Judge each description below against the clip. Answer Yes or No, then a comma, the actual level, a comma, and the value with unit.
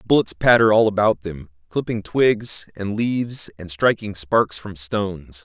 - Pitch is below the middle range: Yes, low, 100 Hz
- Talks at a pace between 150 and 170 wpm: Yes, average, 155 wpm